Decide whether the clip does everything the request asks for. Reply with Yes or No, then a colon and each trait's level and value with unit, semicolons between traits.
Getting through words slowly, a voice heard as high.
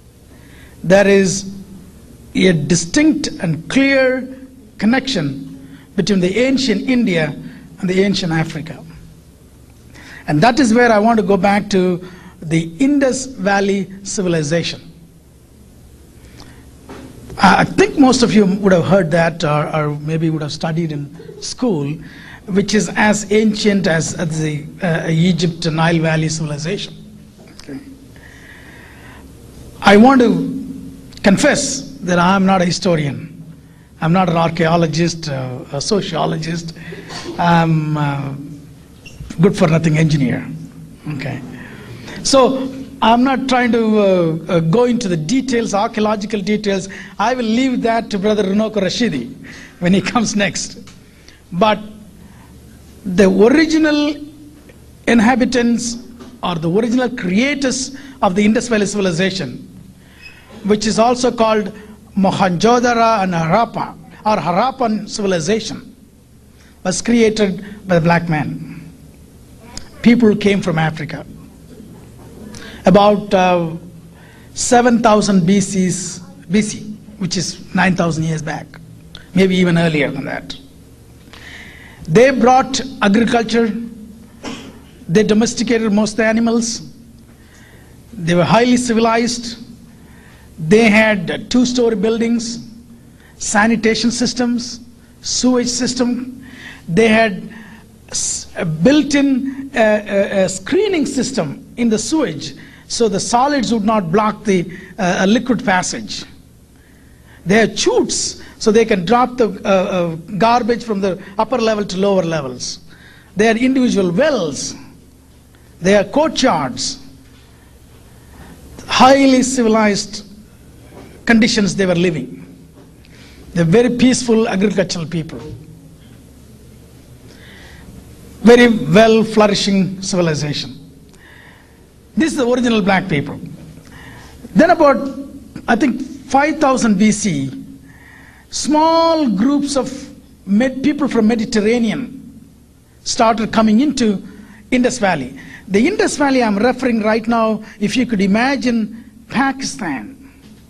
Yes: slow, 110 wpm; high, 210 Hz